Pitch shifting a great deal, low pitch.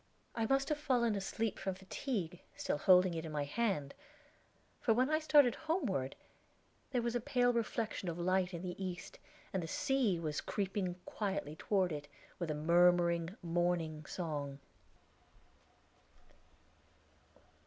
No: wide, 5.7 semitones; medium, 185 Hz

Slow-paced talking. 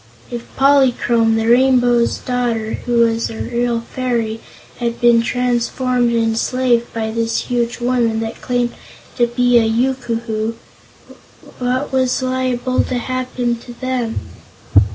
Yes: slow, 130 wpm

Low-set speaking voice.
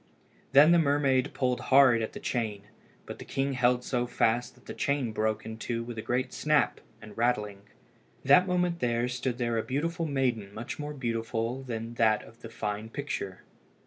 Yes: low, 125 Hz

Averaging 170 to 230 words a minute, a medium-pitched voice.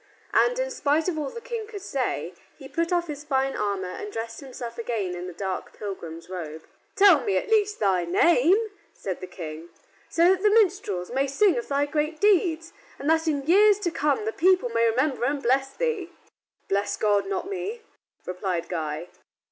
No: average, 190 wpm; very high, 275 Hz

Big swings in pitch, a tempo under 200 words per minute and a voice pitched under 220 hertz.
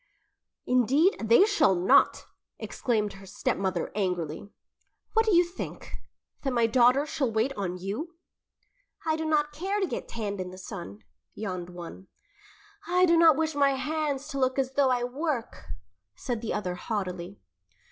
No: wide, 7.7 semitones; average, 155 wpm; very high, 250 Hz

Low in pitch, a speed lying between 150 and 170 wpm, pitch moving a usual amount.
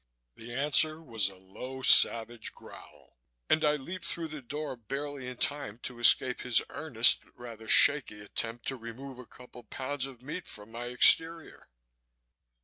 Yes: low, 125 Hz; average, 165 wpm; average, 3.8 semitones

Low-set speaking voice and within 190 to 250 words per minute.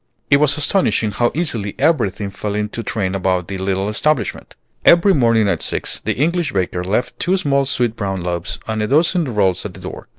Yes: low, 110 Hz; average, 195 wpm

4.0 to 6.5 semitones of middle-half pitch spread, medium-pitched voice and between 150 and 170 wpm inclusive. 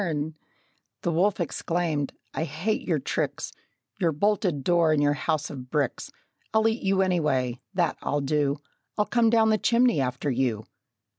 Yes: average, 5.3 semitones; medium, 160 Hz; average, 160 wpm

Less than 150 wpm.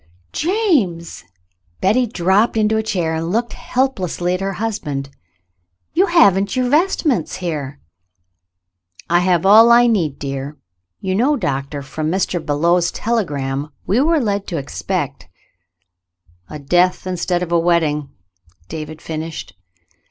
Yes: average, 140 wpm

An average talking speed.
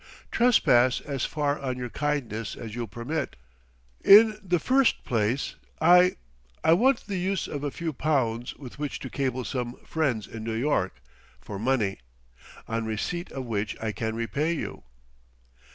Yes: average, 155 wpm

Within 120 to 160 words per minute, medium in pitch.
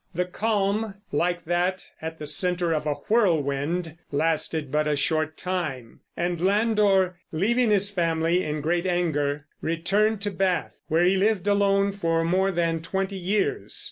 Yes: average, 150 wpm; medium, 175 Hz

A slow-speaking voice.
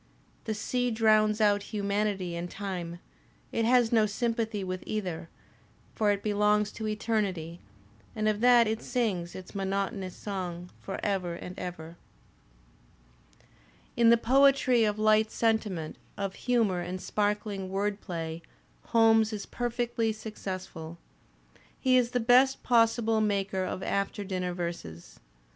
Yes: slow, 130 wpm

